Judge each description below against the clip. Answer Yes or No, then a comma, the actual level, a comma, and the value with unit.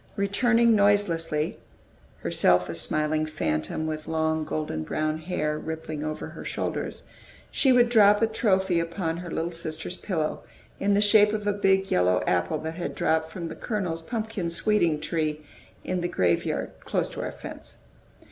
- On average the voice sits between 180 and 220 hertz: No, medium, 165 Hz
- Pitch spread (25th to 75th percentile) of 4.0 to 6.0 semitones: Yes, average, 4.8 semitones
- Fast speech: No, average, 160 wpm